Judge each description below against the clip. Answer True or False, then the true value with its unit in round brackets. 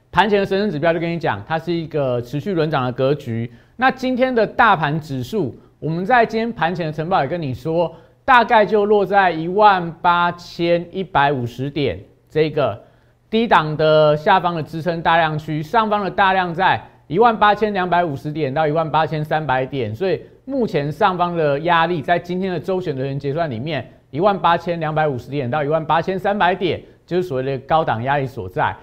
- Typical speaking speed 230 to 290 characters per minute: False (300 characters per minute)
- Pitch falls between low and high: True (165 Hz)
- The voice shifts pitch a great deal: False (4.1 semitones)